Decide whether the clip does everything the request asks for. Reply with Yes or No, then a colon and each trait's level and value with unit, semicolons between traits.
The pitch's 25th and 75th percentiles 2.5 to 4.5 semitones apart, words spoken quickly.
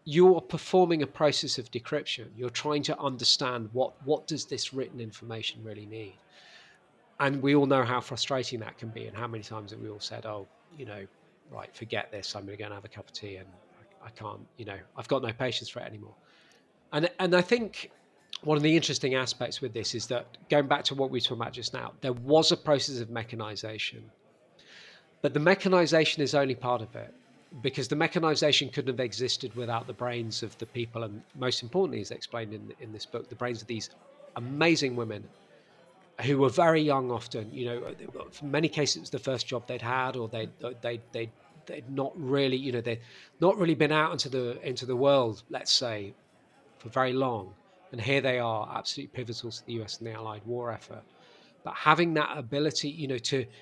Yes: average, 4.1 semitones; fast, 210 wpm